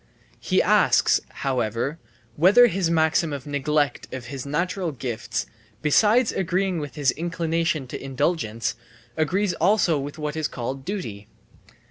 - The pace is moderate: No, slow, 130 wpm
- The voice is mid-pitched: Yes, medium, 155 Hz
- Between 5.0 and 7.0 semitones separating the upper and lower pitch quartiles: No, average, 4.6 semitones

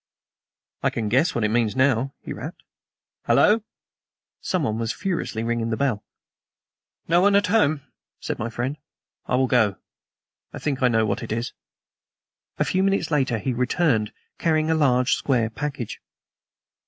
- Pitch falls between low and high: No, low, 130 Hz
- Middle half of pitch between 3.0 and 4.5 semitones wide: No, wide, 5.4 semitones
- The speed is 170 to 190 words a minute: No, average, 155 wpm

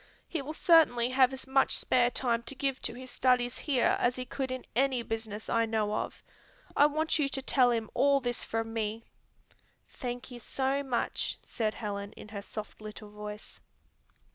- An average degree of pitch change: Yes, average, 3.2 semitones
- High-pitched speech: Yes, high, 245 Hz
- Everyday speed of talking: Yes, average, 185 wpm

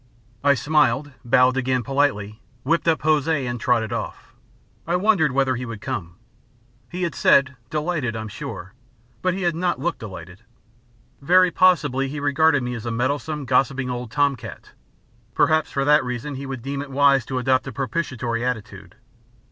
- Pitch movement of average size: Yes, average, 3.7 semitones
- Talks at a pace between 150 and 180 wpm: Yes, average, 170 wpm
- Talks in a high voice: No, low, 135 Hz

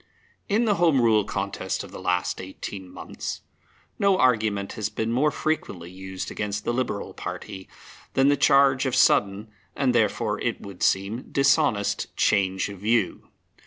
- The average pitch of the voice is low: Yes, low, 105 Hz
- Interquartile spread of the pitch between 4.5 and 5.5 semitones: Yes, average, 5.2 semitones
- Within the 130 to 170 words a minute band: Yes, average, 155 wpm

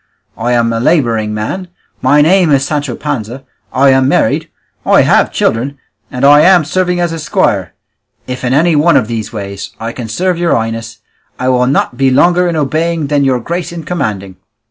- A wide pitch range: Yes, wide, 6.0 semitones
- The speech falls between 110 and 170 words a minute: No, average, 190 wpm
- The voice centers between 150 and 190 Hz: No, low, 135 Hz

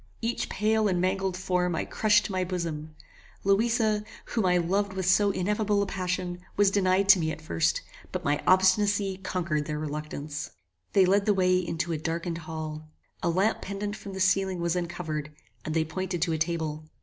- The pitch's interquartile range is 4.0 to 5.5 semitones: No, average, 3.5 semitones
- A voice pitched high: No, medium, 180 Hz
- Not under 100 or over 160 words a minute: No, average, 185 wpm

